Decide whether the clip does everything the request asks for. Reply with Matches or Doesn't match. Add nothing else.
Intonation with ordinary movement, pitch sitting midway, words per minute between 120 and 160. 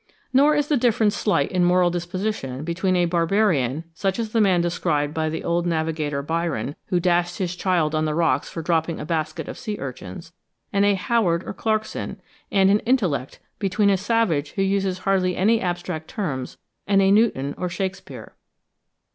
Doesn't match